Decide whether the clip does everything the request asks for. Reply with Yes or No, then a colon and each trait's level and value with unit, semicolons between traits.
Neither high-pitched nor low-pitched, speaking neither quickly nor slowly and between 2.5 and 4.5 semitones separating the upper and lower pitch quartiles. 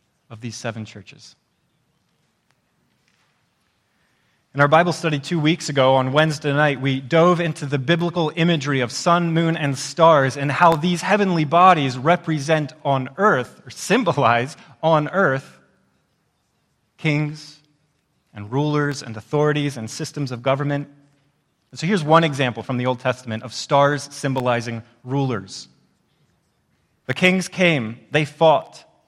No: medium, 145 Hz; slow, 130 wpm; average, 3.6 semitones